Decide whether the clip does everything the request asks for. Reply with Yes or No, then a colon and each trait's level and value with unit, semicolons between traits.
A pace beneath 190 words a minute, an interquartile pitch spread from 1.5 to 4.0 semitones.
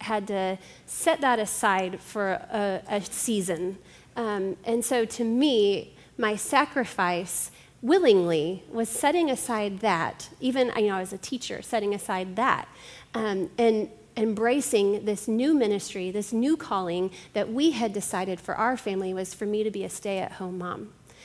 Yes: average, 160 wpm; average, 3.7 semitones